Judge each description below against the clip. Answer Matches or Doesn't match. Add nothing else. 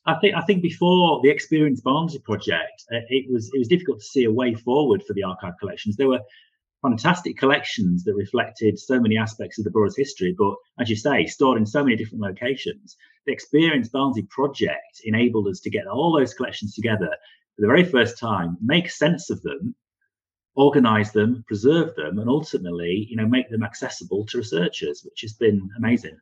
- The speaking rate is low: Doesn't match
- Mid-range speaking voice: Doesn't match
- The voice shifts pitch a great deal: Matches